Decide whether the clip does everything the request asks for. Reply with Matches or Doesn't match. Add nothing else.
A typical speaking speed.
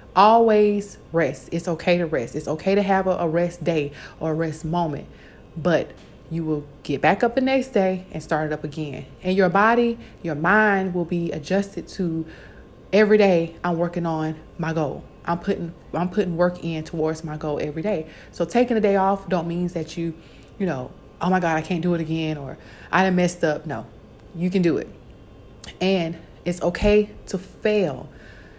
Matches